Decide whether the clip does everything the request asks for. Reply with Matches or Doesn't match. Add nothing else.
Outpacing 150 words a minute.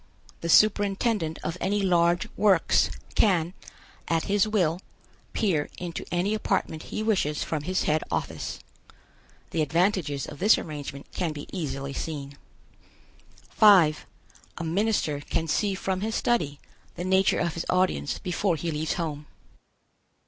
Doesn't match